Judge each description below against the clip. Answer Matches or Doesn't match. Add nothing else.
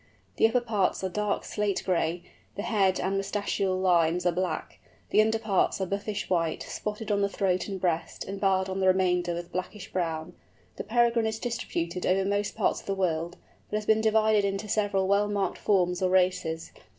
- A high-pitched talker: Matches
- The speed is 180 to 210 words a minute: Matches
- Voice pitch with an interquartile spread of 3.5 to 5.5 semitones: Doesn't match